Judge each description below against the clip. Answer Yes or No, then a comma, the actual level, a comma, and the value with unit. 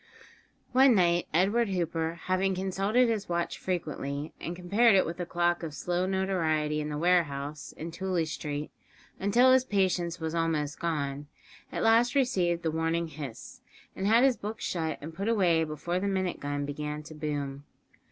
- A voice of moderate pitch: Yes, medium, 170 Hz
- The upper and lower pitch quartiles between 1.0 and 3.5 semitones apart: No, average, 4.0 semitones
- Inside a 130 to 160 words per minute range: No, average, 170 wpm